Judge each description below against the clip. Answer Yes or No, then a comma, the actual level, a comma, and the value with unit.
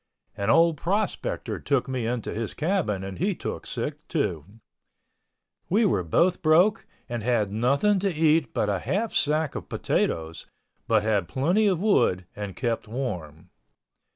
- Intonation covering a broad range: Yes, wide, 8.7 semitones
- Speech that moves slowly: No, average, 155 wpm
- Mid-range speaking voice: No, low, 125 Hz